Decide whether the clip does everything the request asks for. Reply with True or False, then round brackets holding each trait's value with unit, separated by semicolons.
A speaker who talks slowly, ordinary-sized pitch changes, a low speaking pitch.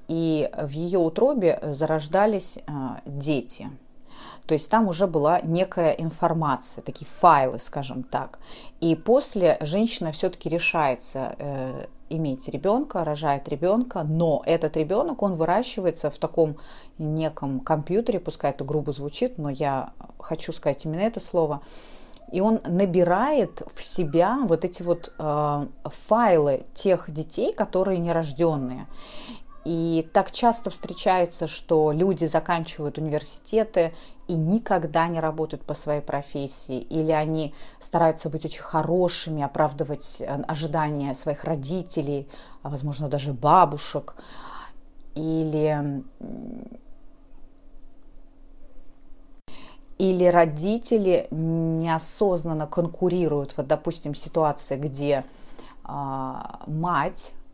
False (105 wpm; 3.8 semitones; 165 Hz)